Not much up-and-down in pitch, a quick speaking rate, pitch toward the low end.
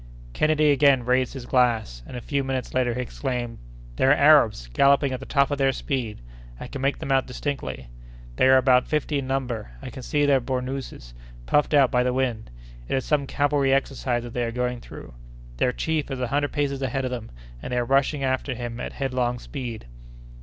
Yes: narrow, 2.1 semitones; fast, 210 wpm; low, 130 Hz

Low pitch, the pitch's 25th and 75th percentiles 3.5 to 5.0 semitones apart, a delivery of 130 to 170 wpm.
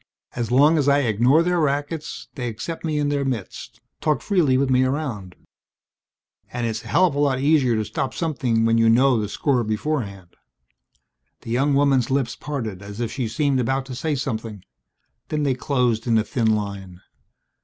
No: low, 130 Hz; average, 4.2 semitones; average, 185 wpm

